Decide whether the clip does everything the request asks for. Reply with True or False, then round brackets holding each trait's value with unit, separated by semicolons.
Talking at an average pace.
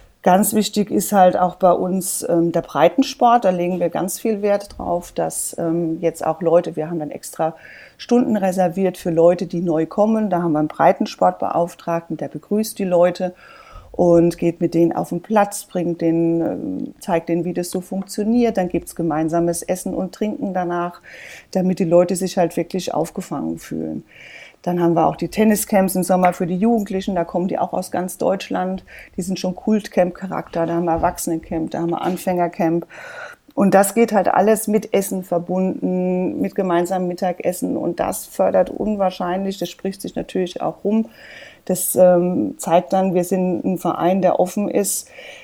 True (180 wpm)